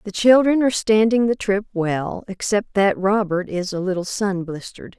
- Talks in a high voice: Yes, high, 200 Hz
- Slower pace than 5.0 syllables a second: Yes, 4.8 syllables/s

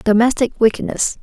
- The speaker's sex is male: No, female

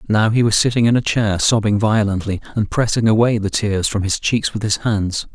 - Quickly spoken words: Yes, fast, 225 wpm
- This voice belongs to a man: Yes, male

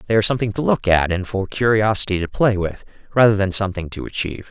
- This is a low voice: Yes, low, 100 Hz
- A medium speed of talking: No, fast, 225 wpm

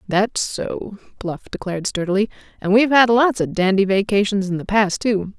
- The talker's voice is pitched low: No, high, 205 Hz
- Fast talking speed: No, average, 180 wpm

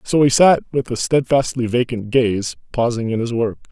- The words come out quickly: No, average, 195 wpm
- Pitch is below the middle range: Yes, low, 125 Hz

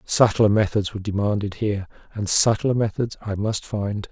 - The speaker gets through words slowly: No, average, 160 wpm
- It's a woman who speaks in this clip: No, male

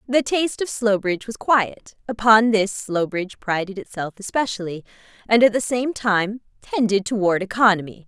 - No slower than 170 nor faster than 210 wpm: No, slow, 135 wpm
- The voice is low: No, high, 210 Hz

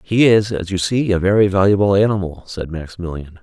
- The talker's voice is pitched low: Yes, very low, 95 Hz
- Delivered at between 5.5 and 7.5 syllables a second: Yes, 5.8 syllables/s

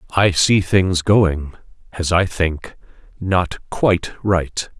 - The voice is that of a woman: No, male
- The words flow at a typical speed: No, slow, 125 wpm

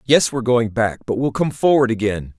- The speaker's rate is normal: No, fast, 225 wpm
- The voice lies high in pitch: No, low, 120 Hz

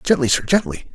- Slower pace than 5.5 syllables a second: No, 5.6 syllables/s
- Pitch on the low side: Yes, low, 130 Hz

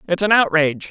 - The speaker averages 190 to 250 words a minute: Yes, average, 200 wpm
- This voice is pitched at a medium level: Yes, medium, 175 Hz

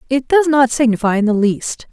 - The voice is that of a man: No, female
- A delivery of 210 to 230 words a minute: Yes, fast, 220 wpm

